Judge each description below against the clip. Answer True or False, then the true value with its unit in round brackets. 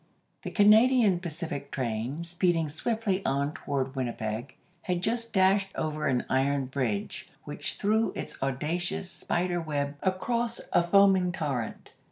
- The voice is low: False (165 Hz)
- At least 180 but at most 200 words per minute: False (135 wpm)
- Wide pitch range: True (5.9 semitones)